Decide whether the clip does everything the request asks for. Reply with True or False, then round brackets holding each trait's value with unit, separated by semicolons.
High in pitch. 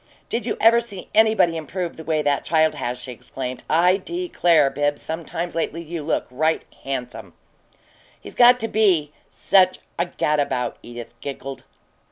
False (160 Hz)